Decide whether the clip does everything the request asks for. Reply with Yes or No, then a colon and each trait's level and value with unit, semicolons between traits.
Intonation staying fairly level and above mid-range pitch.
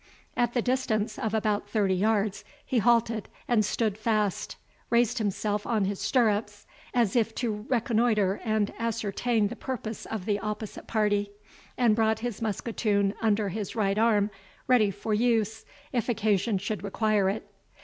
Yes: narrow, 2.0 semitones; high, 215 Hz